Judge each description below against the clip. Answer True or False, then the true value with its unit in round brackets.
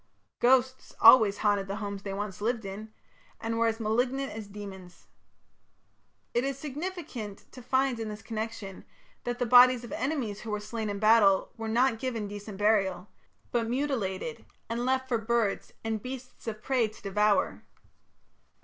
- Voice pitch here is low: False (225 Hz)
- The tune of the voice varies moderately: True (3.2 semitones)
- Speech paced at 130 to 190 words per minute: True (160 wpm)